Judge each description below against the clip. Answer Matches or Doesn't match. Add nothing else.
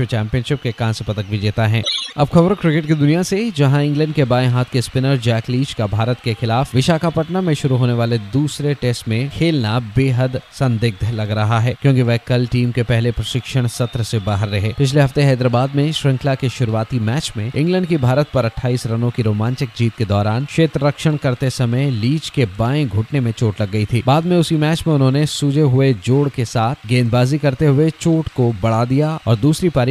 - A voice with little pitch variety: Doesn't match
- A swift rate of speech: Matches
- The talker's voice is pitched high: Doesn't match